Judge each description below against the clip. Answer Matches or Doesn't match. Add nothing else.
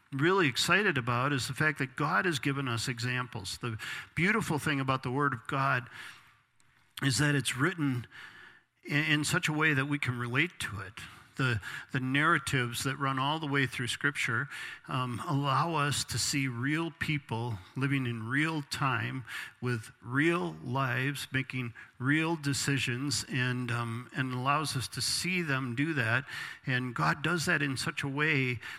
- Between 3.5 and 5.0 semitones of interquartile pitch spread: Doesn't match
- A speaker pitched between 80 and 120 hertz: Doesn't match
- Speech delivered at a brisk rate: Doesn't match